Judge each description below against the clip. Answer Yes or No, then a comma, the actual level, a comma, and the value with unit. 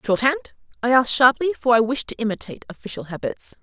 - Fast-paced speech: No, average, 180 wpm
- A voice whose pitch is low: No, high, 245 Hz